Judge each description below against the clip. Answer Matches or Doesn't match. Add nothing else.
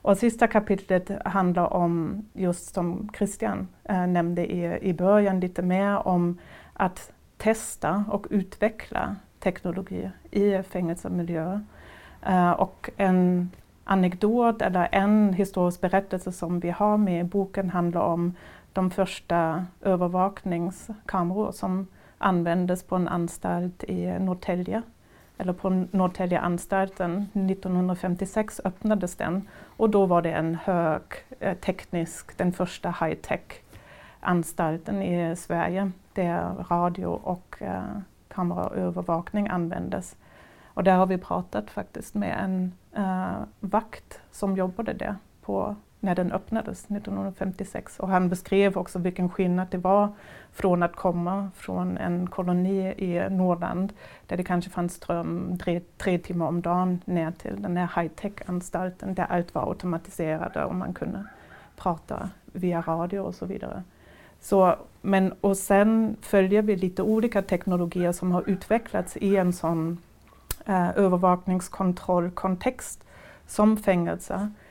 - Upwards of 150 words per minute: Doesn't match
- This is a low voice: Doesn't match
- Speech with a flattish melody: Matches